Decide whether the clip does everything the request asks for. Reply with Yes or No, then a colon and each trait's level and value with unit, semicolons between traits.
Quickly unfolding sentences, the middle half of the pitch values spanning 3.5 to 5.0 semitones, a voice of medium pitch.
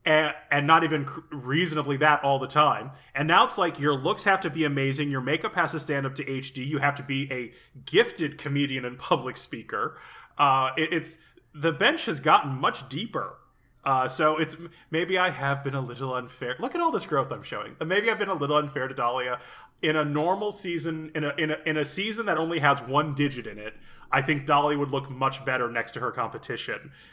No: fast, 220 wpm; average, 3.1 semitones; medium, 150 Hz